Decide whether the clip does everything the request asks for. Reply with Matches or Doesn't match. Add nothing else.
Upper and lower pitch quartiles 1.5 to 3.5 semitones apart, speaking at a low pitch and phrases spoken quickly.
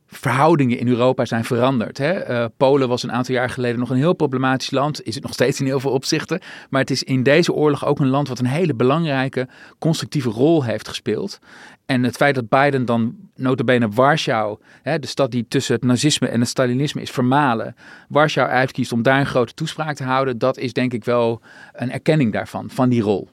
Matches